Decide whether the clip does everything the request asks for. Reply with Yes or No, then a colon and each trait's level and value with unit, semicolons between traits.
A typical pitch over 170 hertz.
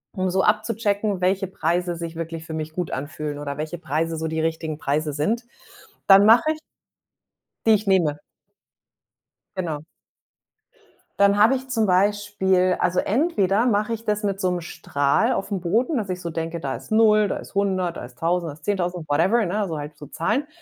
Yes: medium, 185 Hz